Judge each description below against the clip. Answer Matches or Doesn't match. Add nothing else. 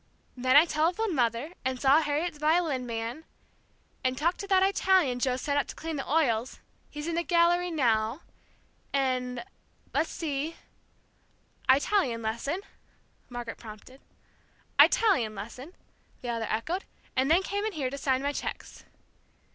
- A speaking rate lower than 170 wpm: Matches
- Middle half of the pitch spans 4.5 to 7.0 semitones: Matches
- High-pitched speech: Matches